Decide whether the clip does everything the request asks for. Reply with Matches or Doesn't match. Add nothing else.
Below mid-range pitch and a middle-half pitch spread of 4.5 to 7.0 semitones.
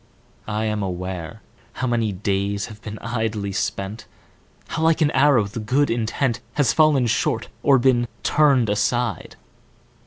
Doesn't match